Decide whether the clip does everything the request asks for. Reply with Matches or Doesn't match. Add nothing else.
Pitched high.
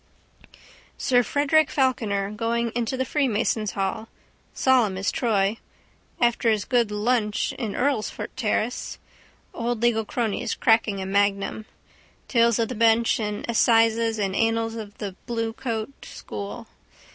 Matches